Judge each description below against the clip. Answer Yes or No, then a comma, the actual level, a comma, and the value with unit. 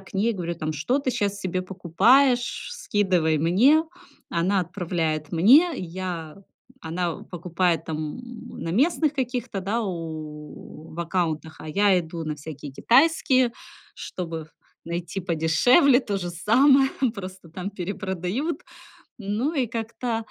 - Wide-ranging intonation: Yes, wide, 6.4 semitones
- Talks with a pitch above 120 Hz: Yes, medium, 185 Hz